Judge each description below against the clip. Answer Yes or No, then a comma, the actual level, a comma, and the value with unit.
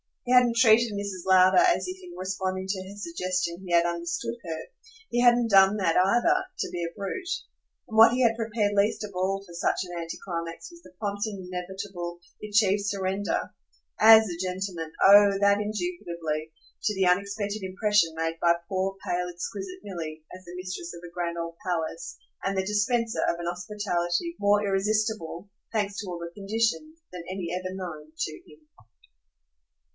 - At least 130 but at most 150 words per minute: No, average, 180 wpm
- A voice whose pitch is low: No, high, 195 Hz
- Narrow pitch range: No, average, 3.4 semitones